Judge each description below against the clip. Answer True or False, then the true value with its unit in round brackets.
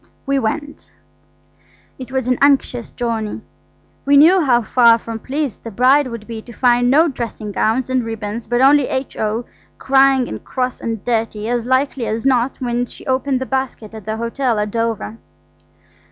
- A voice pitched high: True (245 Hz)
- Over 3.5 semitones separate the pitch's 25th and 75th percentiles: False (2.7 semitones)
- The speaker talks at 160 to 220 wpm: True (170 wpm)